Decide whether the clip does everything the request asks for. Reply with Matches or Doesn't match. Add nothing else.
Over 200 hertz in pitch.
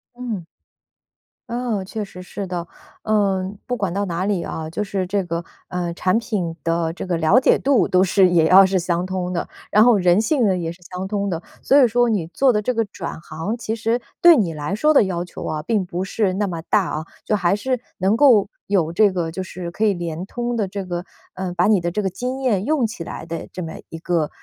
Doesn't match